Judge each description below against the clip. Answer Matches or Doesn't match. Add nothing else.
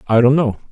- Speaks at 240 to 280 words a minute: Matches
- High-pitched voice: Doesn't match